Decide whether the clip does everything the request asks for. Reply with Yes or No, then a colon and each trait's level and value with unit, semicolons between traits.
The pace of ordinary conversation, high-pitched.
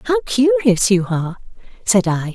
Yes: average, 155 wpm; high, 205 Hz